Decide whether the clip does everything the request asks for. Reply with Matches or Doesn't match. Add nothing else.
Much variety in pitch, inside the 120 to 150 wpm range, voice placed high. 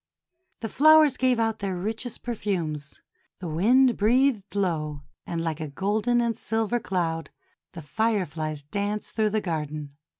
Matches